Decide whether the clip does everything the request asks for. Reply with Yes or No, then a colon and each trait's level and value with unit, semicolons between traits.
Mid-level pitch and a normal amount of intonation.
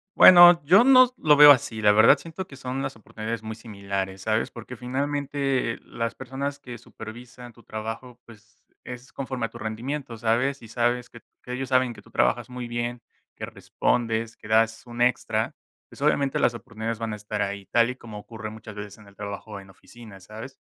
No: low, 120 Hz; average, 3.0 semitones